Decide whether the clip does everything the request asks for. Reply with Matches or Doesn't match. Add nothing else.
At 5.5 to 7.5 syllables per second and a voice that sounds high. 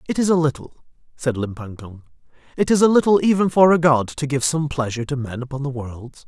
Doesn't match